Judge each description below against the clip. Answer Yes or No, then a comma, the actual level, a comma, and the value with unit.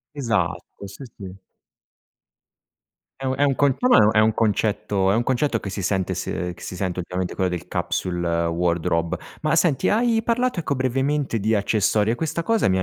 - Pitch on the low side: Yes, low, 110 Hz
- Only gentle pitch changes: No, wide, 7.3 semitones